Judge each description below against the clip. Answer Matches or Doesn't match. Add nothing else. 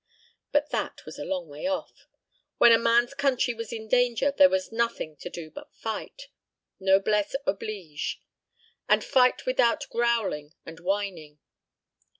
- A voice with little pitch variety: Doesn't match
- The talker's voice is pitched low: Doesn't match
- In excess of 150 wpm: Doesn't match